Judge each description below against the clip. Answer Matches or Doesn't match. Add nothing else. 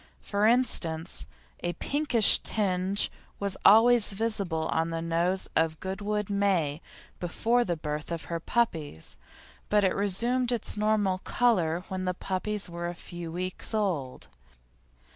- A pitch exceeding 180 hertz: Matches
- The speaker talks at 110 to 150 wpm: Matches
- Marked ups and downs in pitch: Doesn't match